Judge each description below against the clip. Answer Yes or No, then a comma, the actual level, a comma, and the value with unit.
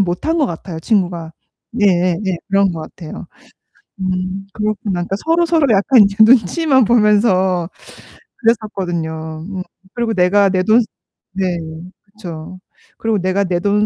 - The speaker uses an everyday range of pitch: Yes, average, 3.3 semitones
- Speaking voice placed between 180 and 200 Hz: Yes, high, 195 Hz